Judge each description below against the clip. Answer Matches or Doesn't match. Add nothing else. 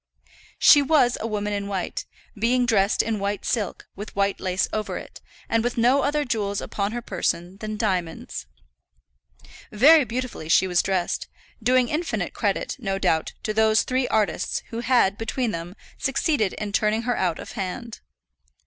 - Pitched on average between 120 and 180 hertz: Doesn't match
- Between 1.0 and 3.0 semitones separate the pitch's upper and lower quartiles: Doesn't match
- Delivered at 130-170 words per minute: Matches